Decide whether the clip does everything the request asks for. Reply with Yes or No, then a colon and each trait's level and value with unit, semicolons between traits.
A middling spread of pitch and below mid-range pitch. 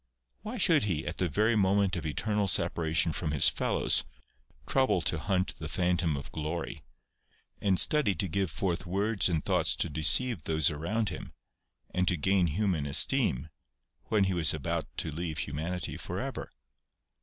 Yes: average, 4.2 semitones; very low, 90 Hz